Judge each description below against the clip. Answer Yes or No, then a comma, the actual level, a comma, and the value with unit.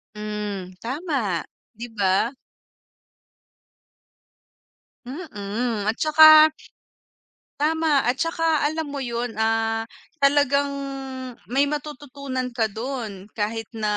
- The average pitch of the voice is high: Yes, very high, 250 Hz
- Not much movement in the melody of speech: No, average, 5.0 semitones